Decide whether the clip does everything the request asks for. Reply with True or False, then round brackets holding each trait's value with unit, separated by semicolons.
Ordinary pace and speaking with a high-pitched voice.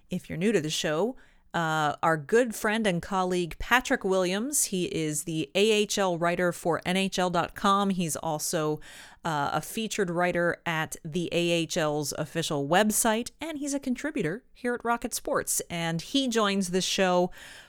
False (155 wpm; 180 Hz)